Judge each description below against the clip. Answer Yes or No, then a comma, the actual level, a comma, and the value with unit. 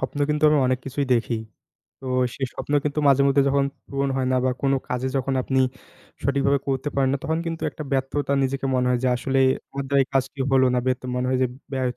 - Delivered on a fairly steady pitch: Yes, narrow, 1.3 semitones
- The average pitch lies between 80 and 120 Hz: No, low, 135 Hz